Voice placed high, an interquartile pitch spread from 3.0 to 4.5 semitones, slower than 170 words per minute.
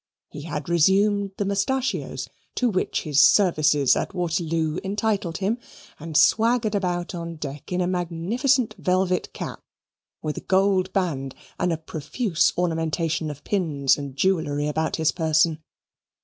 No: medium, 175 Hz; average, 3.9 semitones; average, 140 wpm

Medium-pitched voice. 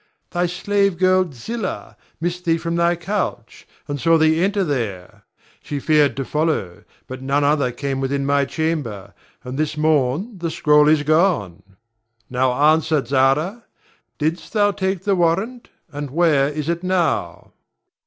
Yes: medium, 155 Hz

